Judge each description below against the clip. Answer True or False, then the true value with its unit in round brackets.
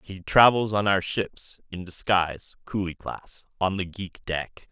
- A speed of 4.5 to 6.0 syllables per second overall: False (4.1 syllables/s)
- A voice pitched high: False (95 Hz)